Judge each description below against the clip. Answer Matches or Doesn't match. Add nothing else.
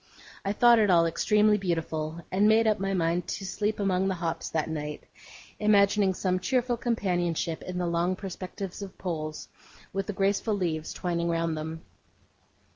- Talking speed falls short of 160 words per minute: Doesn't match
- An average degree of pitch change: Matches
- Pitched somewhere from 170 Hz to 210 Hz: Matches